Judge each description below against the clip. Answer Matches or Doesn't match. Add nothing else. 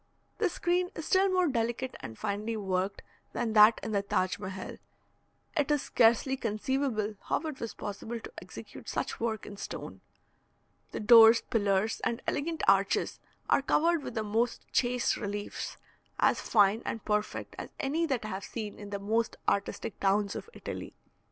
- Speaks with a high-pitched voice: Matches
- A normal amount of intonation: Matches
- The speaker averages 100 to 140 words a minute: Doesn't match